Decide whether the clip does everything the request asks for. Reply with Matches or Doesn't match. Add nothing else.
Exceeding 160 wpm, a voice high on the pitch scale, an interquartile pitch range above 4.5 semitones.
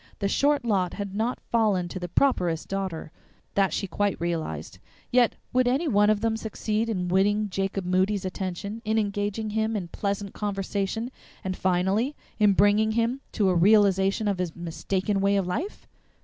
Doesn't match